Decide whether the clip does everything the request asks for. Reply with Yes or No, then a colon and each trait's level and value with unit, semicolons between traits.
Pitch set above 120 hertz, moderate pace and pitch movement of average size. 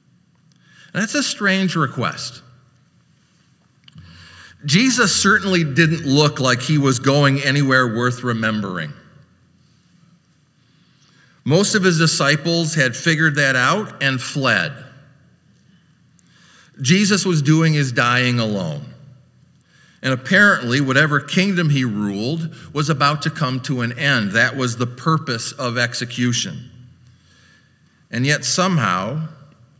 No: medium, 140 Hz; slow, 105 wpm; average, 4.6 semitones